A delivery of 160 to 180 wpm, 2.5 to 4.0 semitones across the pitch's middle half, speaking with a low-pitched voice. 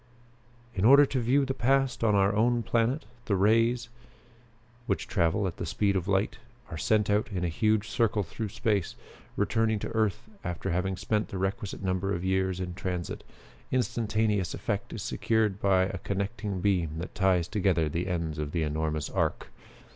Yes: average, 175 wpm; average, 3.5 semitones; low, 100 Hz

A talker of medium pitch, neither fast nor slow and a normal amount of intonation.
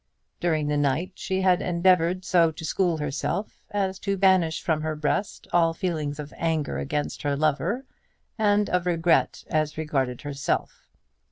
Yes: medium, 165 Hz; average, 155 wpm; average, 3.7 semitones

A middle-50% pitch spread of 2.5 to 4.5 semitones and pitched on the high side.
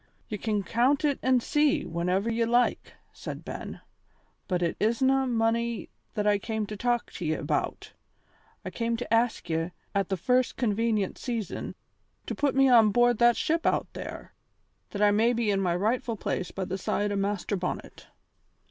Yes: average, 3.4 semitones; high, 225 Hz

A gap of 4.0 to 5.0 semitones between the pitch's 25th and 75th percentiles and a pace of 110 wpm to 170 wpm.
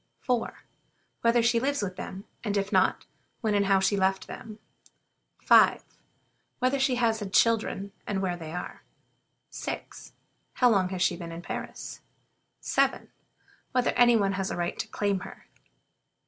No: average, 3.6 semitones; average, 160 wpm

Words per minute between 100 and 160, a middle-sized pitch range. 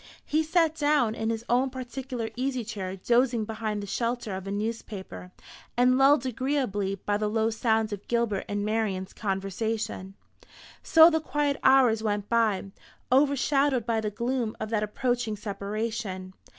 Yes: average, 150 wpm; average, 3.8 semitones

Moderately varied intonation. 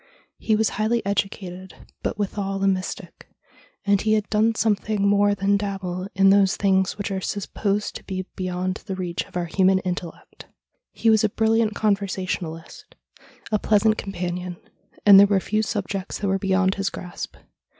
No: narrow, 1.8 semitones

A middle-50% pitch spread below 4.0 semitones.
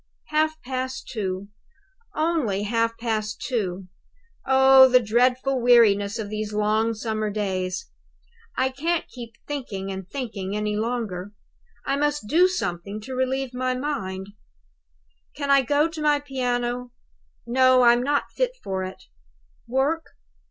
No: average, 4.3 semitones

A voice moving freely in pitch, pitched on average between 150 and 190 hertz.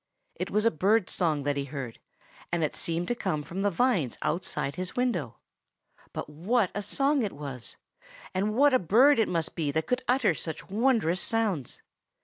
Yes: wide, 6.8 semitones; medium, 185 Hz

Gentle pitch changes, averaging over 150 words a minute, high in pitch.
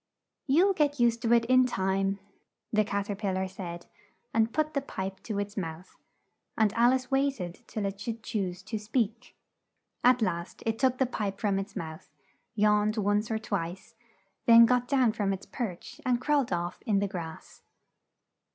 No: average, 3.9 semitones; average, 180 wpm; high, 215 Hz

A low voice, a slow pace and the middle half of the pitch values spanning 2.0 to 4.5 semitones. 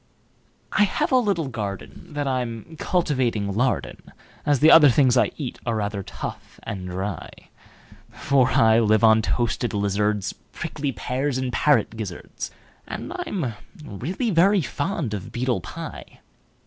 No: low, 125 Hz; slow, 120 wpm; wide, 5.6 semitones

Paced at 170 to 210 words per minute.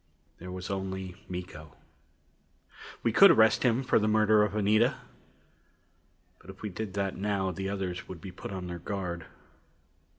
No: average, 160 wpm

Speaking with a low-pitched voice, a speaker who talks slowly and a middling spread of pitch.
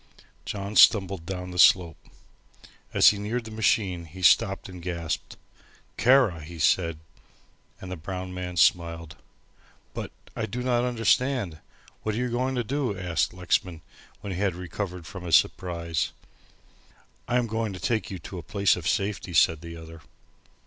No: very low, 95 Hz; average, 165 wpm; average, 4.3 semitones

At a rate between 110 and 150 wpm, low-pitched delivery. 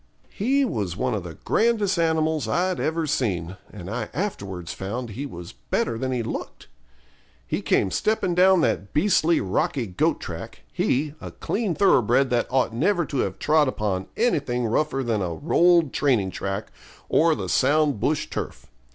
No: average, 165 wpm; low, 130 Hz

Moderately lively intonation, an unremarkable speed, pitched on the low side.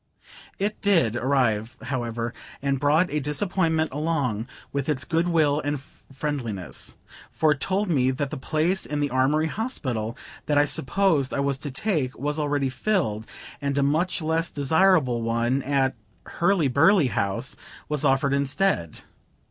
No: average, 3.7 semitones; average, 150 wpm; medium, 145 Hz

